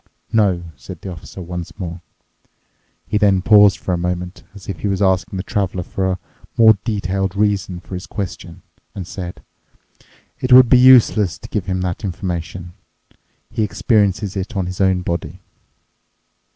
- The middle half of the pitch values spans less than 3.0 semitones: Yes, narrow, 2.4 semitones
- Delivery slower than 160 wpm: No, average, 165 wpm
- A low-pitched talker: Yes, very low, 95 Hz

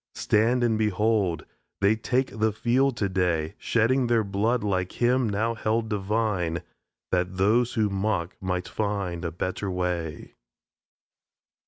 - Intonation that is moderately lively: Yes, average, 3.7 semitones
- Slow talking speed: Yes, slow, 130 wpm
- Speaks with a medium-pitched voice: No, low, 105 Hz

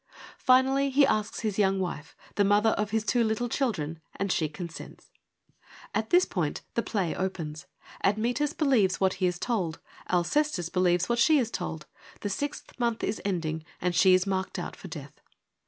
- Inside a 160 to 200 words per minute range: Yes, average, 175 wpm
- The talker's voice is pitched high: Yes, high, 200 Hz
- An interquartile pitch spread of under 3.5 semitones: No, average, 5.0 semitones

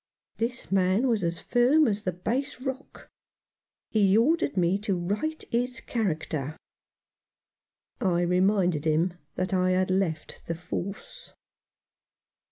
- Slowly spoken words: Yes, slow, 120 wpm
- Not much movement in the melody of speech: No, average, 5.0 semitones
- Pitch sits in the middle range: No, high, 195 Hz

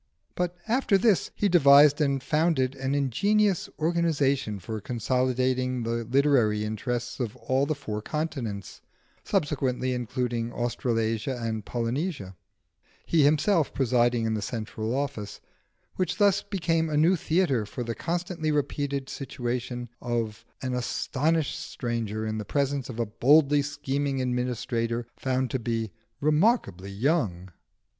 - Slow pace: Yes, slow, 130 wpm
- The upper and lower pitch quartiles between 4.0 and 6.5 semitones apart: Yes, average, 4.4 semitones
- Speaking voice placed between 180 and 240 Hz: No, low, 130 Hz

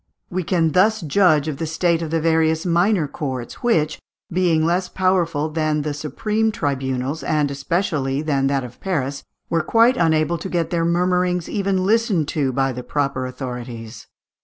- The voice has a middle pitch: Yes, medium, 160 Hz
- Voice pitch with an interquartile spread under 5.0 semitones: Yes, average, 4.3 semitones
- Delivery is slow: No, average, 165 wpm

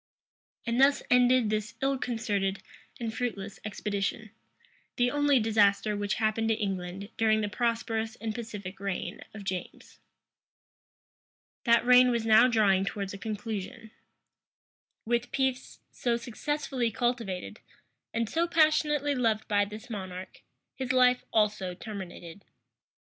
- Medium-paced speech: No, slow, 125 wpm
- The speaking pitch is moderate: No, high, 220 Hz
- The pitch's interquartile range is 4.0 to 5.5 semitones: No, average, 3.3 semitones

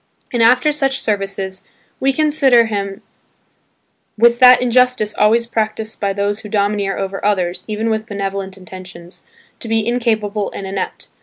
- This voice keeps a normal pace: Yes, average, 145 wpm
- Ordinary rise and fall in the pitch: Yes, average, 3.2 semitones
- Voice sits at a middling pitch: No, high, 215 Hz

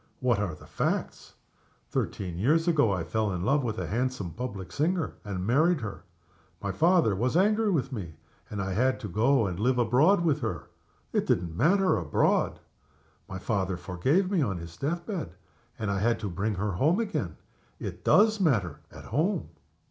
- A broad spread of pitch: Yes, wide, 8.5 semitones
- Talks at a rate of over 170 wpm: Yes, average, 180 wpm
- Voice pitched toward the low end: Yes, low, 115 Hz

